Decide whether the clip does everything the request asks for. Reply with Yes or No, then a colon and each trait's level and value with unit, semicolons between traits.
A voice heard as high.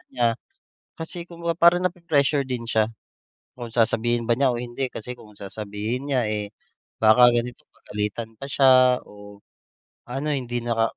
No: low, 120 Hz